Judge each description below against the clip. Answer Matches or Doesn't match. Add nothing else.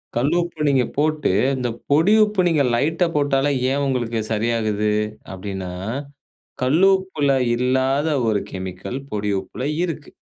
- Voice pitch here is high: Doesn't match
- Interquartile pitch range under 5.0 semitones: Doesn't match